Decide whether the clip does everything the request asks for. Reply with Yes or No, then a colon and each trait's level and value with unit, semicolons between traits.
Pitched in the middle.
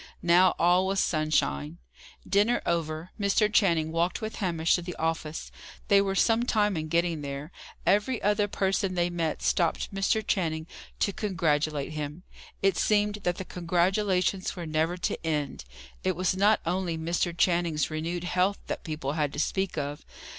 Yes: medium, 175 Hz